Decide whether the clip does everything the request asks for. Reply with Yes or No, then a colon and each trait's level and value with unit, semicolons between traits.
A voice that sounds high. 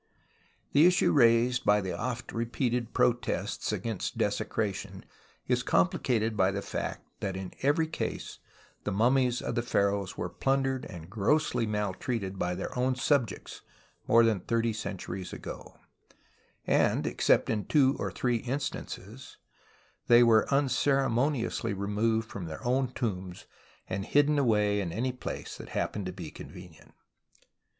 No: low, 115 Hz